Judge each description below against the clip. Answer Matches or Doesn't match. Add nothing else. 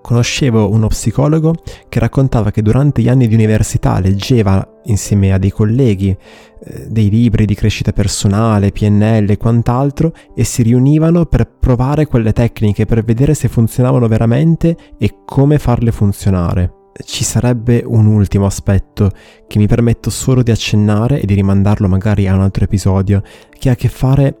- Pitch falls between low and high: Doesn't match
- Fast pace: Doesn't match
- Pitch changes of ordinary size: Matches